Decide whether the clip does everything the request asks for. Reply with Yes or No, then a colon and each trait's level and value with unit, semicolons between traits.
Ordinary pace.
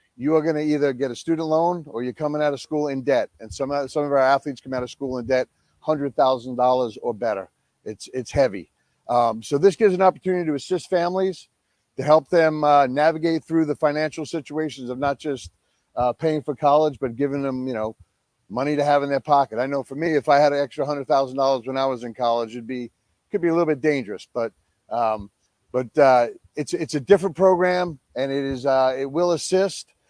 No: fast, 230 wpm